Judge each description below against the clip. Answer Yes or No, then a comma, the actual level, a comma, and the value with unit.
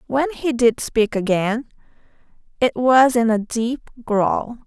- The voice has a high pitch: Yes, high, 240 Hz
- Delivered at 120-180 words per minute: Yes, average, 140 wpm